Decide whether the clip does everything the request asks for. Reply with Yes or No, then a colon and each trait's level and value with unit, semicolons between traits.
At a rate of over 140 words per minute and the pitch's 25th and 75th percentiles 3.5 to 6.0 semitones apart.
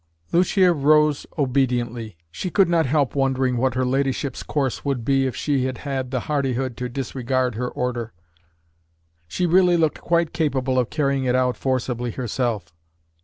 No: average, 155 wpm; average, 2.8 semitones